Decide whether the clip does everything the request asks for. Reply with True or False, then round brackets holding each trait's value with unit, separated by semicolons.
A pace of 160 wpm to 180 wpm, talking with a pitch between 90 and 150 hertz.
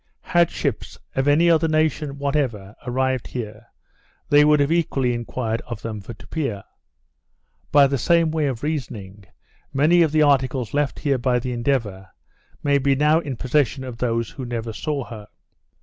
True (165 wpm; 135 Hz)